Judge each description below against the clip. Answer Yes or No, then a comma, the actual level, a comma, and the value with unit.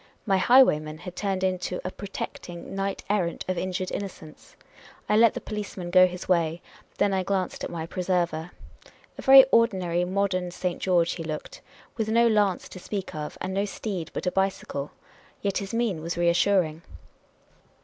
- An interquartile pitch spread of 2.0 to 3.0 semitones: Yes, narrow, 2.5 semitones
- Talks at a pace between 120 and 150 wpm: No, average, 170 wpm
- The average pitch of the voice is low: No, medium, 185 Hz